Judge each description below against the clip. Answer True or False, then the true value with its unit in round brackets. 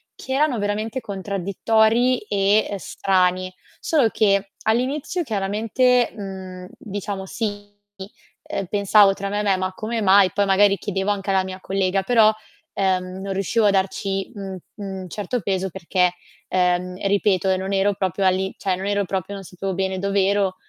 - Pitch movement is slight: True (1.5 semitones)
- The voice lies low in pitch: False (195 Hz)